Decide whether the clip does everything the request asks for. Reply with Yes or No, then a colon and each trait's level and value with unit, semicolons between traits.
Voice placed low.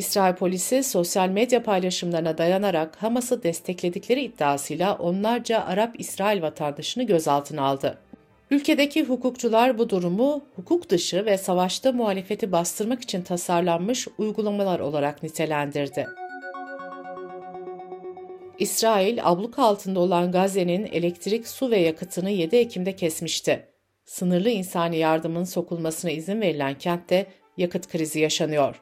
No: medium, 185 Hz